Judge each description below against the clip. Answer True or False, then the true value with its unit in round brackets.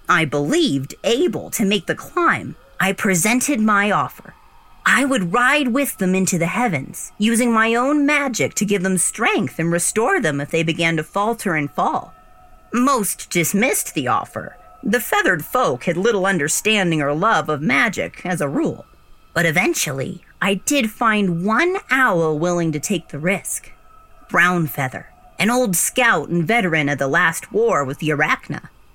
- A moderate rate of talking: True (165 wpm)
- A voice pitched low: False (190 Hz)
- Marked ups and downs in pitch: True (6.4 semitones)